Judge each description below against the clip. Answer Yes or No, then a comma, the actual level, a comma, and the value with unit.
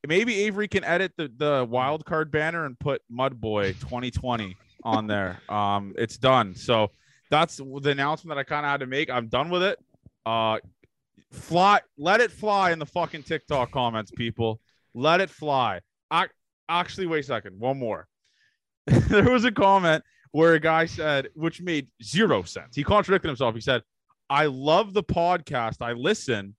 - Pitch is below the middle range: No, medium, 145 Hz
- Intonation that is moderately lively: No, wide, 5.7 semitones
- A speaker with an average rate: Yes, average, 175 wpm